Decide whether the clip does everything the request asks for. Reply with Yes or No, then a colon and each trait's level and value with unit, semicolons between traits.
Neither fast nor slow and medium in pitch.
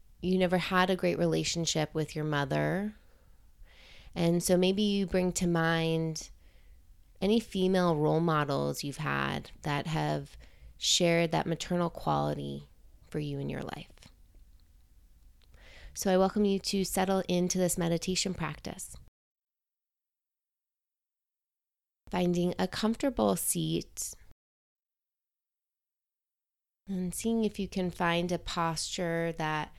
No: slow, 115 wpm; medium, 165 Hz